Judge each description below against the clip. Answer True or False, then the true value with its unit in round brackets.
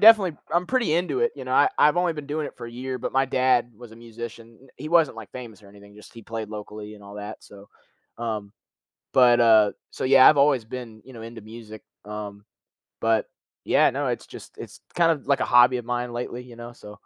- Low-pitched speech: True (120 Hz)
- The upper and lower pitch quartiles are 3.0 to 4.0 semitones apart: True (3.6 semitones)